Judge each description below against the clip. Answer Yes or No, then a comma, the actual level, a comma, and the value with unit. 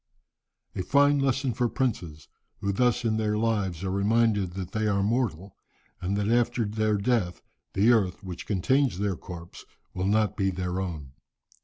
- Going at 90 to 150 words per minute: No, average, 165 wpm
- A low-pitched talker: Yes, low, 105 Hz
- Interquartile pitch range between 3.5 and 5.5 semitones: Yes, average, 3.9 semitones